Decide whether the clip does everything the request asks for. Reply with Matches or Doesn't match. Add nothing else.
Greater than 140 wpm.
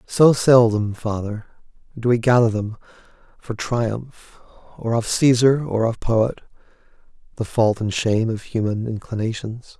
Doesn't match